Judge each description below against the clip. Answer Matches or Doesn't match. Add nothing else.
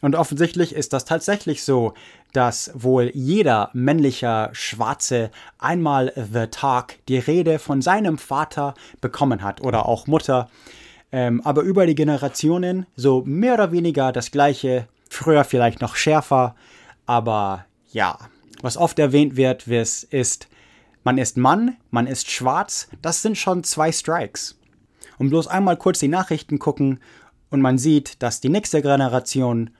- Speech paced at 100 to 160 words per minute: Matches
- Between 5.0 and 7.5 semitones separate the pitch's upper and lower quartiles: Doesn't match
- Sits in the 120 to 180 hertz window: Matches